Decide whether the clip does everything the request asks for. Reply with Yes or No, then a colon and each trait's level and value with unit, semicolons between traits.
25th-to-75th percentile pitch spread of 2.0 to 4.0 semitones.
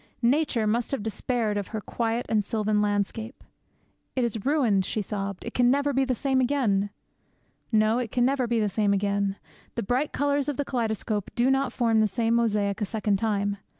Yes: average, 3.5 semitones